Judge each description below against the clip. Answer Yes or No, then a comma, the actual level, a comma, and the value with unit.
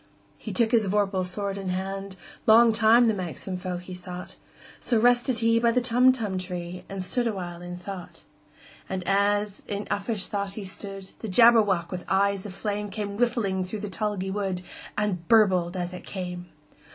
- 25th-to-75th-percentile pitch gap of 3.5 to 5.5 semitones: No, average, 2.9 semitones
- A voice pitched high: Yes, high, 195 Hz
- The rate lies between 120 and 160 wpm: Yes, average, 150 wpm